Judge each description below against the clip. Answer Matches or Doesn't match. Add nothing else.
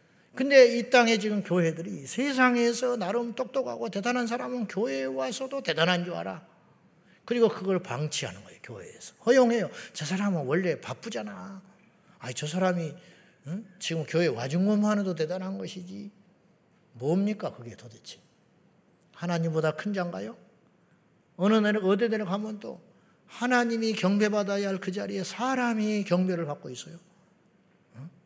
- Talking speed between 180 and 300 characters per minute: Doesn't match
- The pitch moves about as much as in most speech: Matches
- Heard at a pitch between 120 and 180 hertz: Doesn't match